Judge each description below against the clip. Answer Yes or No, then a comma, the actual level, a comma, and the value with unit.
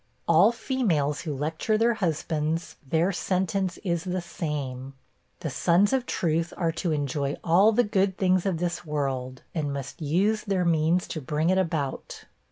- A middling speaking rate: Yes, average, 165 wpm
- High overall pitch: No, medium, 170 Hz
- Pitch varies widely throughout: No, average, 4.0 semitones